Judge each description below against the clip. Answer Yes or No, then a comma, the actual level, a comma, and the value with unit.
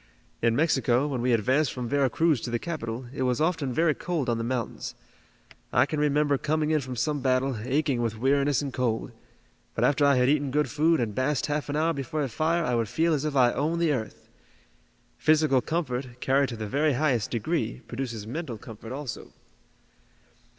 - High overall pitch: No, low, 135 Hz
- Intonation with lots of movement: No, average, 3.8 semitones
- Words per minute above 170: Yes, average, 200 wpm